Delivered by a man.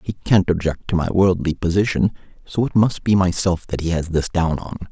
Yes: male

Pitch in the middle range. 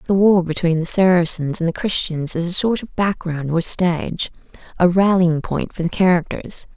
Yes: medium, 175 Hz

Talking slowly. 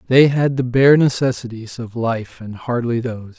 No: average, 175 wpm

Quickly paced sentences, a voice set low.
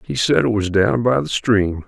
Yes: fast, 255 wpm; low, 110 Hz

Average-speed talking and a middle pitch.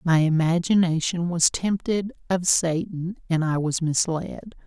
No: slow, 130 wpm; medium, 170 Hz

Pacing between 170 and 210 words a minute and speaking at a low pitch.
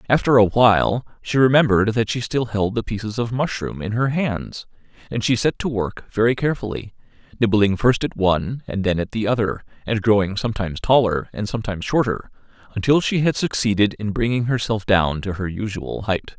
Yes: average, 185 wpm; low, 110 Hz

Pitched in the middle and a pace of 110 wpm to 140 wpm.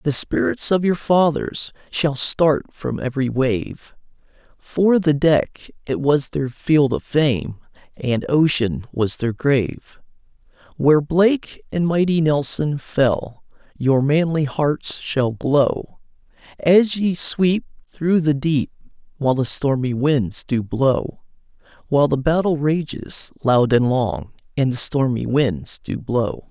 Yes: medium, 145 Hz; slow, 135 wpm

